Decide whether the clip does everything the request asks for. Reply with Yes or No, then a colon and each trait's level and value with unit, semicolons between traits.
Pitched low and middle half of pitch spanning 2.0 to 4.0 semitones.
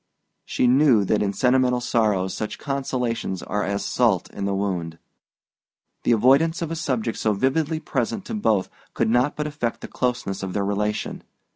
No: low, 120 Hz; average, 5.0 semitones